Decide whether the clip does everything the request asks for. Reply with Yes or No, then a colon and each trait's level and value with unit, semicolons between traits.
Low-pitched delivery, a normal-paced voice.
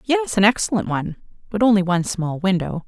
No: high, 200 Hz; average, 190 wpm